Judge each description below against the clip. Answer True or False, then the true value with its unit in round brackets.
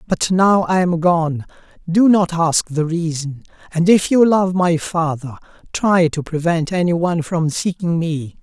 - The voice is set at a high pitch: False (170 Hz)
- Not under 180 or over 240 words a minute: False (170 wpm)